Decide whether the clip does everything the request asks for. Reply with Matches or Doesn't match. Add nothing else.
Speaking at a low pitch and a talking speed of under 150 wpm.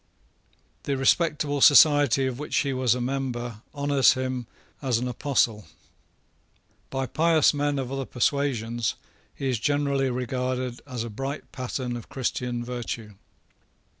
Matches